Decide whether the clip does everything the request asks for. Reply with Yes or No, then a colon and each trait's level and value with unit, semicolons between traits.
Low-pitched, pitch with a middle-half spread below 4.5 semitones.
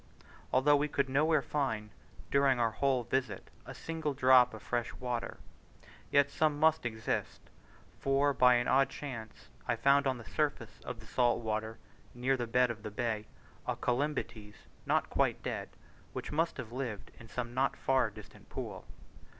Yes: low, 125 Hz; average, 3.3 semitones